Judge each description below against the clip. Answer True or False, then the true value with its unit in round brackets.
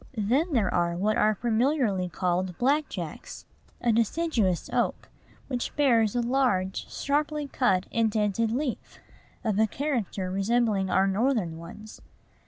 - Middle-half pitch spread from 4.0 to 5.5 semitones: True (5.1 semitones)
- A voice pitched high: True (220 Hz)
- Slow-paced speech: True (130 wpm)